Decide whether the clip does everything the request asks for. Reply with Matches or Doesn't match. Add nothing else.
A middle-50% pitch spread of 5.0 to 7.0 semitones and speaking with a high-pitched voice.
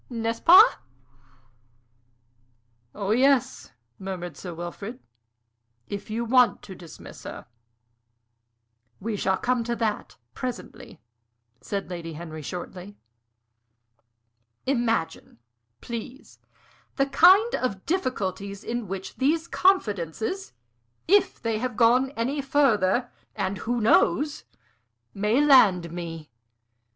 Matches